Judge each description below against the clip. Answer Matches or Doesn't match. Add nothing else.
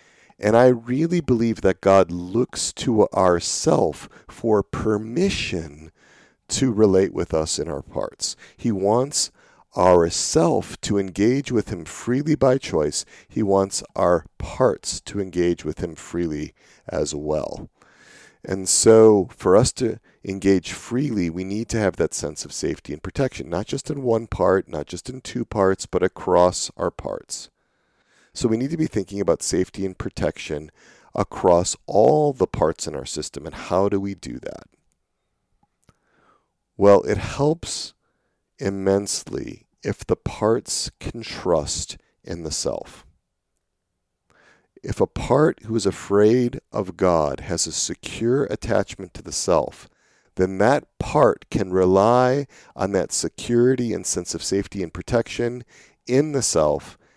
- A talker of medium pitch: Doesn't match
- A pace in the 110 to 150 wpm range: Matches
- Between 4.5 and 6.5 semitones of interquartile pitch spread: Matches